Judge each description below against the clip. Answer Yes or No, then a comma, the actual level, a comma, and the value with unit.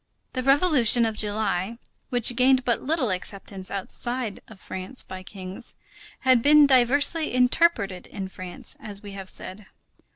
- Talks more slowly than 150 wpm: Yes, average, 140 wpm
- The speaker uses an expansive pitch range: No, average, 5.0 semitones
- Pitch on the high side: Yes, high, 230 Hz